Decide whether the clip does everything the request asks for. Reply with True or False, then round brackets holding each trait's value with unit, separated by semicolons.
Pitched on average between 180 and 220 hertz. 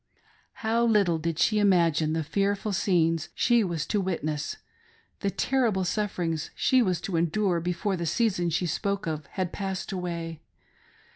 True (185 Hz)